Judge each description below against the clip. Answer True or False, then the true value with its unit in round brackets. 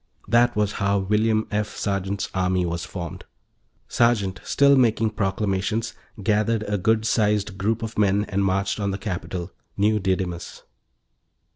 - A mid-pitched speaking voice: False (105 Hz)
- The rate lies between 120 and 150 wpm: True (140 wpm)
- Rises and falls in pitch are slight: True (2.3 semitones)